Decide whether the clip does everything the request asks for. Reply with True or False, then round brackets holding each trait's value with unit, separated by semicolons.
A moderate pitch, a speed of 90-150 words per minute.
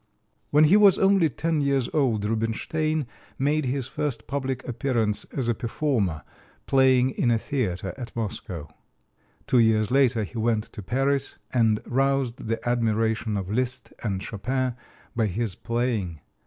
False (120 Hz; 145 wpm)